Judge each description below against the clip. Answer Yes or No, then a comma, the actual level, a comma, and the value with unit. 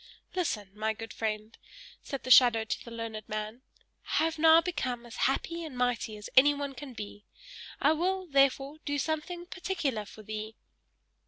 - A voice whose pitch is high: Yes, very high, 255 Hz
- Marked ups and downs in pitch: Yes, wide, 6.1 semitones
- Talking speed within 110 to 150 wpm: No, average, 165 wpm